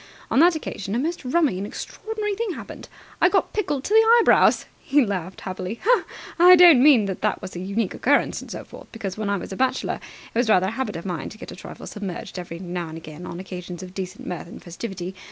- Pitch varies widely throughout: Yes, wide, 7.8 semitones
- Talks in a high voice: Yes, high, 200 Hz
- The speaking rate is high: Yes, fast, 235 wpm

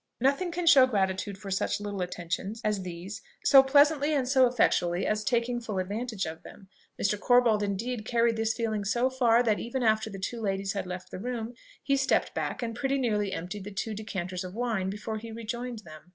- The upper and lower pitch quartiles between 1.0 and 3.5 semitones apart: No, average, 4.0 semitones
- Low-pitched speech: No, high, 220 Hz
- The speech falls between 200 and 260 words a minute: Yes, fast, 205 wpm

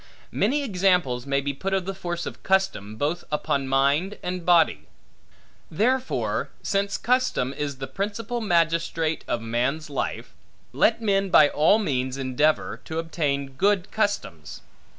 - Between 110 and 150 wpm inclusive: Yes, average, 140 wpm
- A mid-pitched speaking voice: Yes, medium, 165 Hz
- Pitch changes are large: Yes, wide, 6.0 semitones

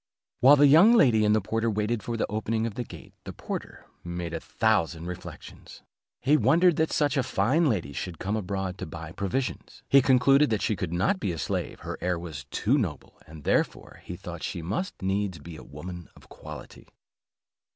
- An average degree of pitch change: No, wide, 7.1 semitones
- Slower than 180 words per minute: No, average, 195 wpm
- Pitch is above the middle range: No, low, 105 Hz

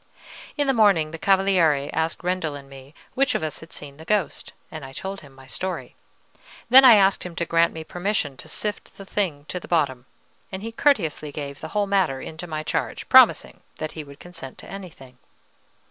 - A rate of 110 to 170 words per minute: No, fast, 205 wpm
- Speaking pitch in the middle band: Yes, medium, 165 Hz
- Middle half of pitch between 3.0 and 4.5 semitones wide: No, average, 5.1 semitones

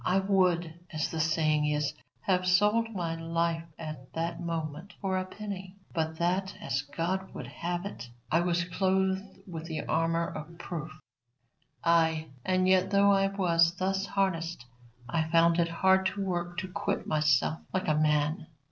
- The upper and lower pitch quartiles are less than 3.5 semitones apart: Yes, average, 2.7 semitones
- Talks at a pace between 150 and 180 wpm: Yes, average, 155 wpm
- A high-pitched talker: No, medium, 170 Hz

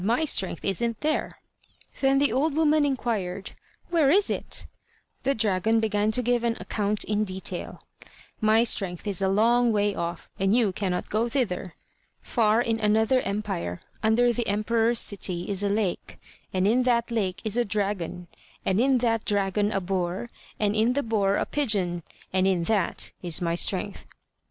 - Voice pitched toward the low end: No, high, 215 Hz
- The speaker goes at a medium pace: Yes, average, 165 wpm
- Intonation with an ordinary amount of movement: Yes, average, 3.6 semitones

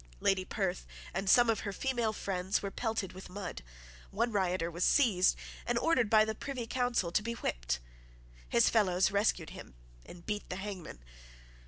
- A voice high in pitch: Yes, high, 200 Hz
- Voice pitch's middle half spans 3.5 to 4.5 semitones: Yes, average, 3.8 semitones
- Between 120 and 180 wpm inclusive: Yes, average, 170 wpm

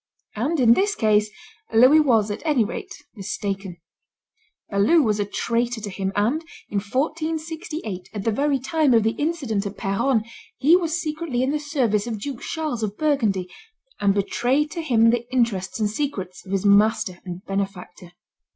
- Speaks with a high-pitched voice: Yes, high, 230 Hz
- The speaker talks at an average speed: Yes, average, 170 wpm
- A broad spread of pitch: Yes, wide, 6.5 semitones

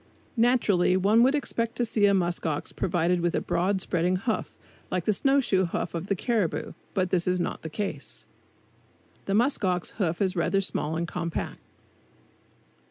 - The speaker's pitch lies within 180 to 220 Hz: Yes, medium, 185 Hz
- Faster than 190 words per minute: No, average, 175 wpm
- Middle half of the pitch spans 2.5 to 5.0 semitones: Yes, average, 3.3 semitones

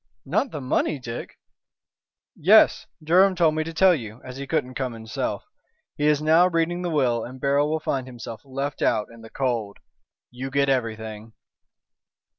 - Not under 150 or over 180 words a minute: Yes, average, 170 wpm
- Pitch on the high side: No, low, 135 Hz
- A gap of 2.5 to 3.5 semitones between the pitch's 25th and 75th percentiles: No, average, 4.7 semitones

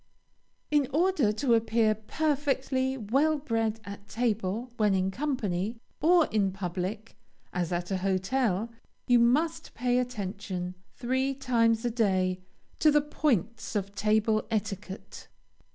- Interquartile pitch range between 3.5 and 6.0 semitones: Yes, average, 4.8 semitones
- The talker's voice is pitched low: No, high, 225 Hz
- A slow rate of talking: Yes, slow, 125 wpm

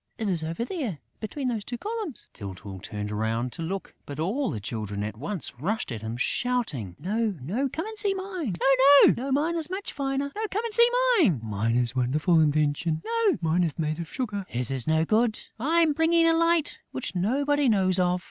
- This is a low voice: No, high, 190 Hz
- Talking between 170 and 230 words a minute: Yes, average, 185 wpm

